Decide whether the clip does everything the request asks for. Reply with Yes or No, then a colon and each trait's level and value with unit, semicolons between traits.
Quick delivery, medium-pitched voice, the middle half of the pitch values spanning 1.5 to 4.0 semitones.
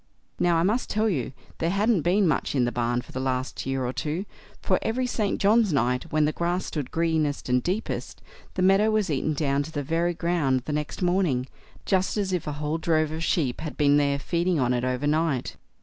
No: fast, 220 wpm; medium, 160 Hz; average, 4.7 semitones